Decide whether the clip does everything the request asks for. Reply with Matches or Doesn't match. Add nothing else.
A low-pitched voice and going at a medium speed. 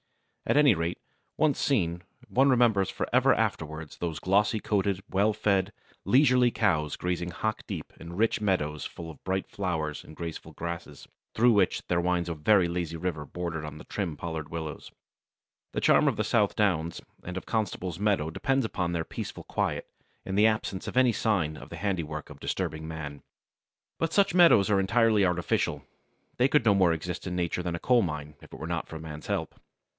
Matches